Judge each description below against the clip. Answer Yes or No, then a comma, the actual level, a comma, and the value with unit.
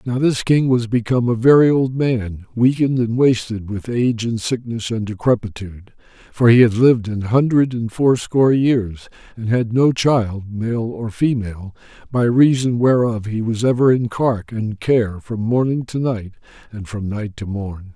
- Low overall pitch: Yes, low, 115 Hz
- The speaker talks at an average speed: Yes, average, 175 wpm